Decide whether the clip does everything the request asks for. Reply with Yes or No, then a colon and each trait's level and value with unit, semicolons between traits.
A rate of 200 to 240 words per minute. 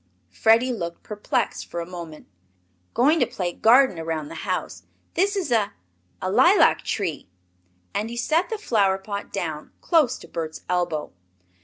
No: average, 155 wpm